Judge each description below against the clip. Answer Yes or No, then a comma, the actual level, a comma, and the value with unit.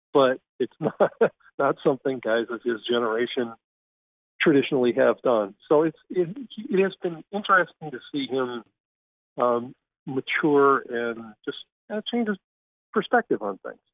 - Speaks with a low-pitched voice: Yes, low, 130 Hz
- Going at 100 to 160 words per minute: Yes, average, 140 wpm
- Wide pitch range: Yes, wide, 6.6 semitones